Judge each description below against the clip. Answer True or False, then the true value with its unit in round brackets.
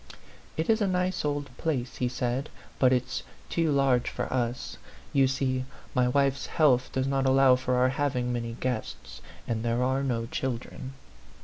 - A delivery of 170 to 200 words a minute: True (180 wpm)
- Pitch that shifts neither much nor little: False (1.9 semitones)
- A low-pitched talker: True (130 Hz)